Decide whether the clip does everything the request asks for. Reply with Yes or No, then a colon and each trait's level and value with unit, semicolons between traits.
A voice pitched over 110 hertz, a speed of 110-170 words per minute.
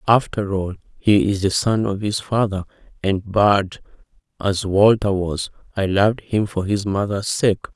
No: low, 100 Hz; average, 165 wpm